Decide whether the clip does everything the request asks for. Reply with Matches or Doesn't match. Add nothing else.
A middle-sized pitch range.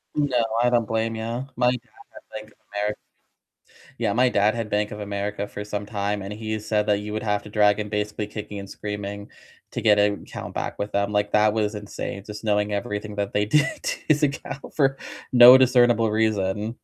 Doesn't match